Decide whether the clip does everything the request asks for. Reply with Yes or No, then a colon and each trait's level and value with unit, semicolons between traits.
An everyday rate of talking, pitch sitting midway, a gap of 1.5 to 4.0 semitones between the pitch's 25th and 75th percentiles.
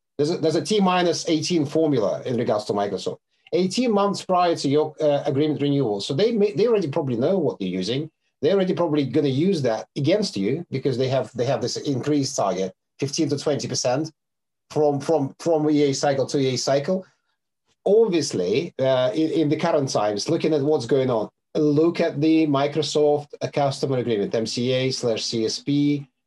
Yes: average, 180 wpm; medium, 150 Hz; average, 2.8 semitones